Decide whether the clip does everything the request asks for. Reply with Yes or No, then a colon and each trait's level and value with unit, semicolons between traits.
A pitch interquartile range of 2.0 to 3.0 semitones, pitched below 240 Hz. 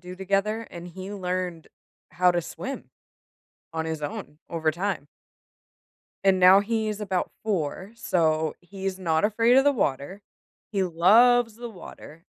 No: average, 4.0 semitones; medium, 185 Hz